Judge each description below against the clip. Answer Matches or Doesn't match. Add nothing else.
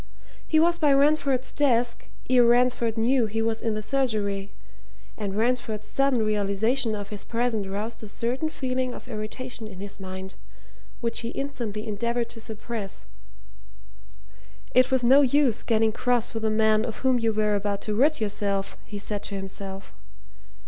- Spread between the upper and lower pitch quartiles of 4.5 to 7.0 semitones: Doesn't match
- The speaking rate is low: Doesn't match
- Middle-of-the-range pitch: Doesn't match